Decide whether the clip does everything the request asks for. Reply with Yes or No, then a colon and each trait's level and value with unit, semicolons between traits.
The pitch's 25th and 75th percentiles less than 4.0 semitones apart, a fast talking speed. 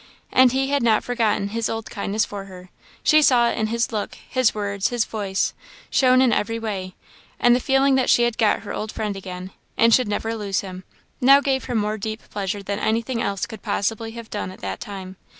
Yes: average, 3.1 semitones; fast, 220 wpm